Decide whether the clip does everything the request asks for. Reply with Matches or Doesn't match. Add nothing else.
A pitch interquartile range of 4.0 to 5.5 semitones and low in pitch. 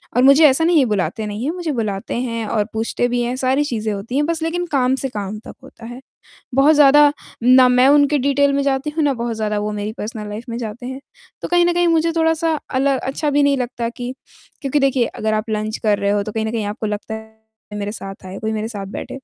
Doesn't match